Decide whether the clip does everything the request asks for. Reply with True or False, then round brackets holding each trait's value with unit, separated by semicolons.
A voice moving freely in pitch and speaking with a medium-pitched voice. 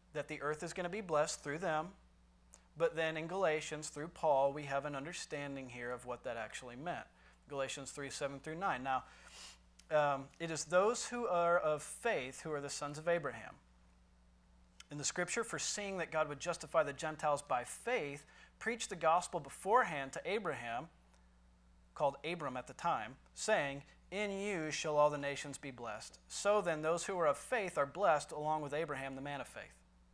False (3.7 semitones; 145 Hz)